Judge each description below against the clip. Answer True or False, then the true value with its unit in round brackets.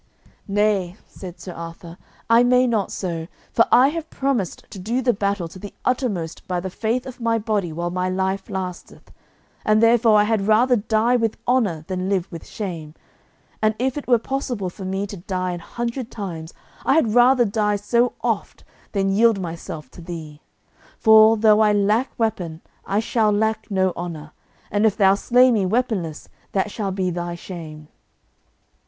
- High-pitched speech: True (205 Hz)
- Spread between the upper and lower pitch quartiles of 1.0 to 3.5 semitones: False (4.1 semitones)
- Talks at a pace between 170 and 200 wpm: True (175 wpm)